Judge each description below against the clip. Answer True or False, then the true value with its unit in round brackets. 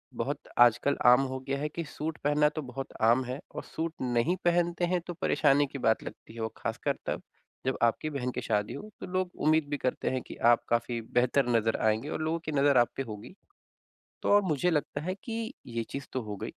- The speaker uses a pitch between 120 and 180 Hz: True (140 Hz)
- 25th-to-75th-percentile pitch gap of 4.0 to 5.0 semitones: True (4.6 semitones)